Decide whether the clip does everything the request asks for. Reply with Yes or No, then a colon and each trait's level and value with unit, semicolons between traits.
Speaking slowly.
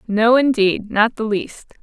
Yes: slow, 130 wpm